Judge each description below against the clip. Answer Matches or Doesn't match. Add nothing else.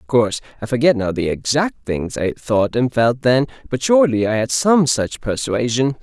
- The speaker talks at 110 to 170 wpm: Doesn't match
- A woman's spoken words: Doesn't match